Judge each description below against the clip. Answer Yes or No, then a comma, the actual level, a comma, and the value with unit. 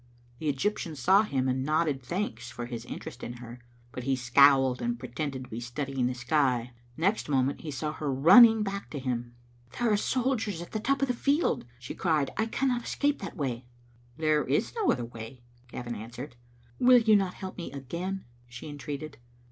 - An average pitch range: No, wide, 7.7 semitones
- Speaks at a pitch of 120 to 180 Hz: Yes, medium, 140 Hz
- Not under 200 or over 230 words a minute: Yes, fast, 205 wpm